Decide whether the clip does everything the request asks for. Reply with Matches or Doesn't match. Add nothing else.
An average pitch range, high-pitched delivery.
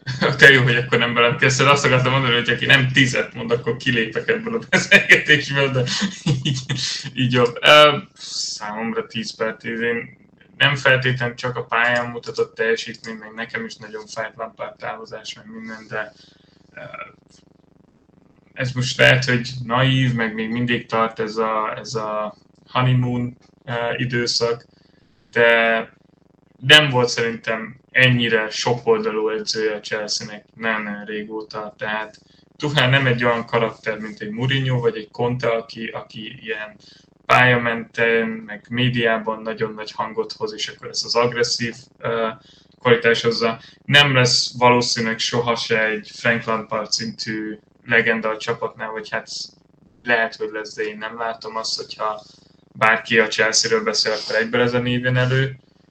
Doesn't match